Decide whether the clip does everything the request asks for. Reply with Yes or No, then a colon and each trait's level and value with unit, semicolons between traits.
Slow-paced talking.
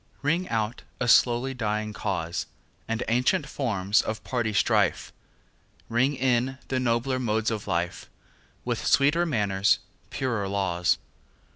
Yes: slow, 125 wpm